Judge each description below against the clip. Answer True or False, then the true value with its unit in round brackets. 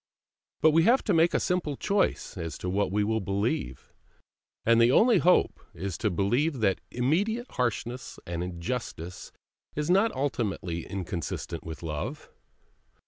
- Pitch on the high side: False (115 Hz)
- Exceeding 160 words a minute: False (145 wpm)